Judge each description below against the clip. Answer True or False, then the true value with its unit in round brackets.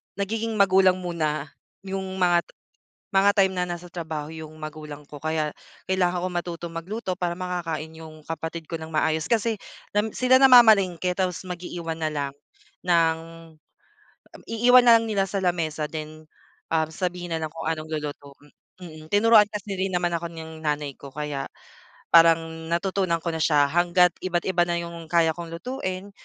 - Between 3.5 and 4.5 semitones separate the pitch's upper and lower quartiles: False (2.9 semitones)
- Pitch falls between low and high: True (170 Hz)